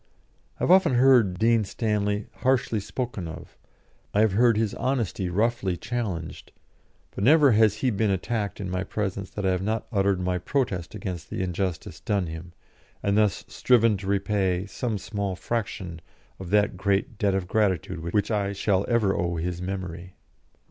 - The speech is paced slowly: No, average, 170 wpm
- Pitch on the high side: No, low, 100 Hz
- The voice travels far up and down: No, average, 3.2 semitones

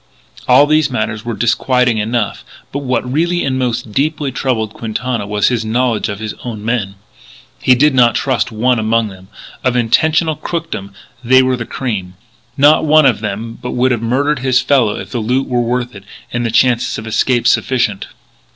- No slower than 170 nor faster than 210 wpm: Yes, average, 185 wpm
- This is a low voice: Yes, low, 120 Hz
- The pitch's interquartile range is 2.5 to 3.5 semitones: Yes, average, 2.9 semitones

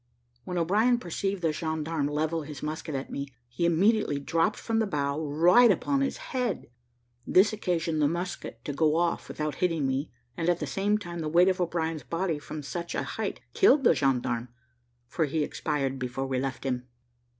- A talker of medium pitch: Yes, medium, 160 Hz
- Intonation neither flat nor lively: Yes, average, 4.1 semitones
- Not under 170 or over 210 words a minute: Yes, average, 185 wpm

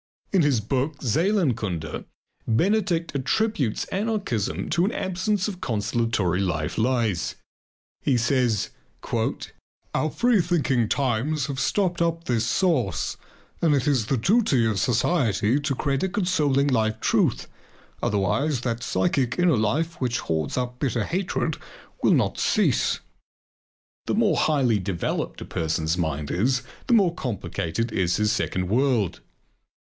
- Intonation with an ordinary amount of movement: No, wide, 7.5 semitones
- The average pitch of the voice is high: No, low, 130 Hz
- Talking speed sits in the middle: No, slow, 130 wpm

